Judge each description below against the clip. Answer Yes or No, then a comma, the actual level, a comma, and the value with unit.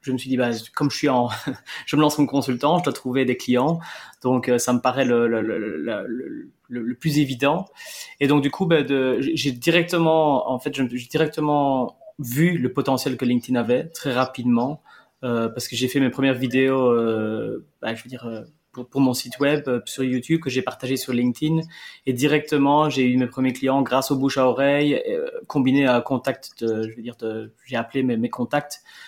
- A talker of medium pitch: No, low, 130 Hz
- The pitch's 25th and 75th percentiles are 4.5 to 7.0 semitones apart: No, average, 2.9 semitones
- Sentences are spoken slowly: No, average, 215 wpm